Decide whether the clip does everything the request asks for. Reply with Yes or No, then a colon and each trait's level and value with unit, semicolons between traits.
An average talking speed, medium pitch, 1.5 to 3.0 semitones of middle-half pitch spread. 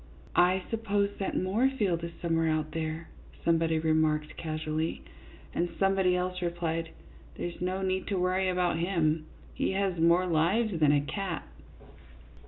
Yes: average, 155 wpm; medium, 175 Hz; average, 2.7 semitones